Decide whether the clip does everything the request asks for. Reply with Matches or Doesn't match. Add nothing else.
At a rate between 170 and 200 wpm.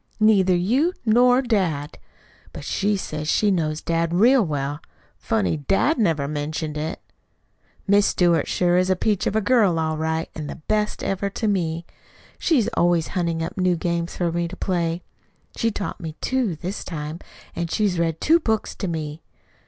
Matches